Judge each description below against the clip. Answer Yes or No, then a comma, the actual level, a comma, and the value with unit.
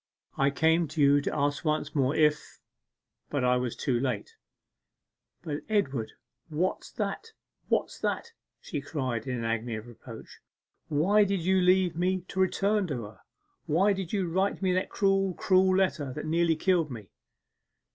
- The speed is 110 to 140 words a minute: No, average, 165 wpm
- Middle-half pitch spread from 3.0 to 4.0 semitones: No, wide, 5.6 semitones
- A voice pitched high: No, medium, 160 Hz